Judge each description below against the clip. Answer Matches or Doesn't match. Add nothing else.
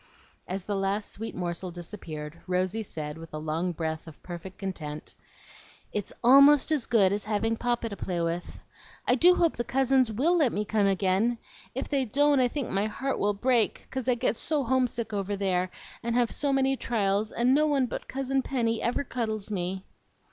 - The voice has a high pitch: Matches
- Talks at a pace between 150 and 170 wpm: Doesn't match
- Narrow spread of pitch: Doesn't match